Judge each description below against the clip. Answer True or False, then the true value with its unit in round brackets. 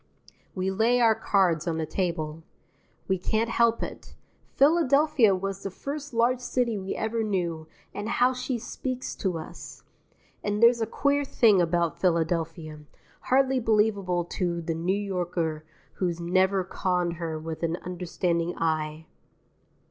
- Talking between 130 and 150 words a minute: True (145 wpm)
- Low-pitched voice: False (190 Hz)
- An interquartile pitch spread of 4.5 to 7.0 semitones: True (5.4 semitones)